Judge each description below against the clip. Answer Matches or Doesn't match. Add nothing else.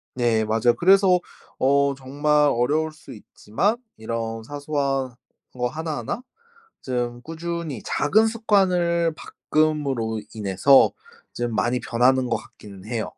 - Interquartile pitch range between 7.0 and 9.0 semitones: Doesn't match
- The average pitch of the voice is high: Doesn't match